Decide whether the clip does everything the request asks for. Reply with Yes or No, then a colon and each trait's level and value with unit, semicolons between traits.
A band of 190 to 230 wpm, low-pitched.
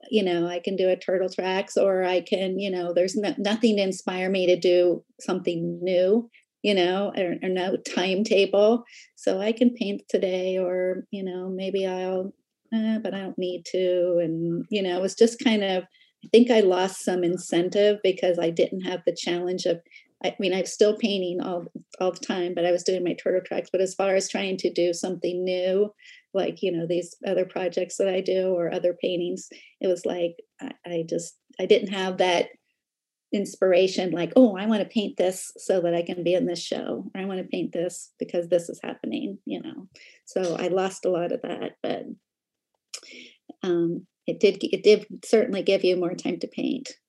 No: fast, 205 wpm; medium, 185 Hz